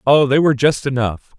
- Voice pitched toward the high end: No, low, 135 Hz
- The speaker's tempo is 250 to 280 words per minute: No, fast, 215 wpm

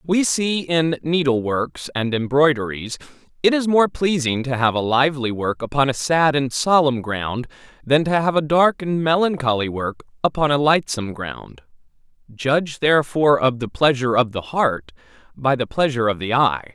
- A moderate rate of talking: Yes, average, 170 wpm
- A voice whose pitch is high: No, medium, 140 Hz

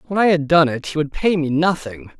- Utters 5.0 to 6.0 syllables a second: Yes, 5.6 syllables/s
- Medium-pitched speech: Yes, medium, 160 Hz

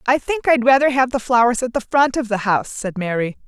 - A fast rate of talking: Yes, fast, 275 wpm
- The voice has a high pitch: Yes, high, 245 Hz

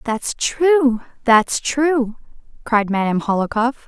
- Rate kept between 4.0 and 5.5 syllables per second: No, 3.6 syllables/s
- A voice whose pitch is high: Yes, high, 245 Hz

